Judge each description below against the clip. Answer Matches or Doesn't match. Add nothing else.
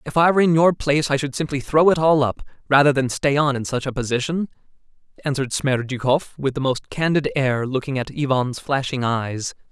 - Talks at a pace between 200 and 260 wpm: Matches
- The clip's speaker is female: Doesn't match